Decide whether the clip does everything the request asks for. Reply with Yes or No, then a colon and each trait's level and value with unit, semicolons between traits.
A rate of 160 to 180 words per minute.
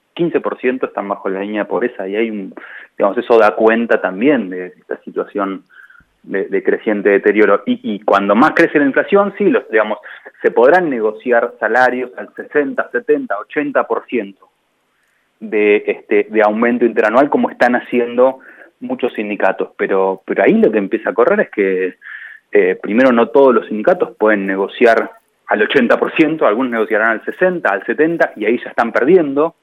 Yes: average, 165 wpm